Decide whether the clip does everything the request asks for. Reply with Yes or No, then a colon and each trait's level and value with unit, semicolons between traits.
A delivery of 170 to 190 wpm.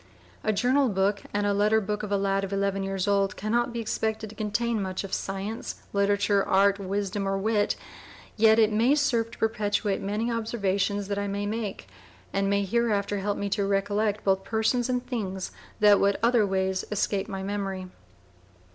Yes: average, 185 wpm